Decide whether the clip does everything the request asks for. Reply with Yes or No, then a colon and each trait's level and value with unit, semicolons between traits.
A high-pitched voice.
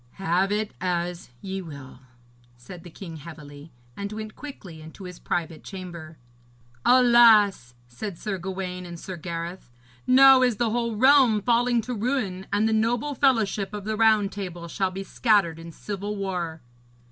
Yes: high, 195 Hz